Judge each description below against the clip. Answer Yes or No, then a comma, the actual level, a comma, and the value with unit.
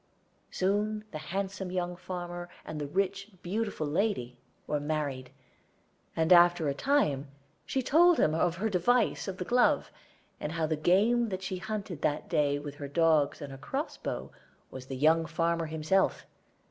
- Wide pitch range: No, average, 4.6 semitones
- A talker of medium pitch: Yes, medium, 175 Hz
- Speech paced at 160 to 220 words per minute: Yes, average, 170 wpm